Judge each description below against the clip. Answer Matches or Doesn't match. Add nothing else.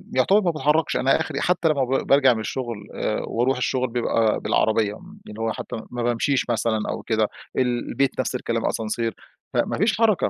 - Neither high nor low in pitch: Doesn't match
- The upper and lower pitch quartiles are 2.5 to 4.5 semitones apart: Matches